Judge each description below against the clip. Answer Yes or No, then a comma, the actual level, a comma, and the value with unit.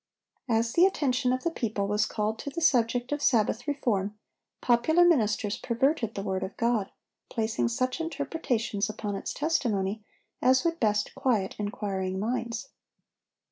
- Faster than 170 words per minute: No, average, 145 wpm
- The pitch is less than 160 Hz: No, high, 230 Hz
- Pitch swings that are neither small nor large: Yes, average, 4.1 semitones